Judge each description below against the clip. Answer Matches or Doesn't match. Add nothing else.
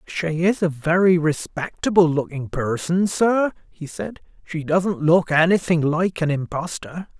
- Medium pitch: Matches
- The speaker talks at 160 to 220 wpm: Doesn't match